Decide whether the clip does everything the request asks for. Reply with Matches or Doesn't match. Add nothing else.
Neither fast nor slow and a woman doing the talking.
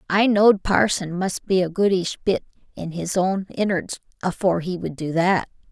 Matches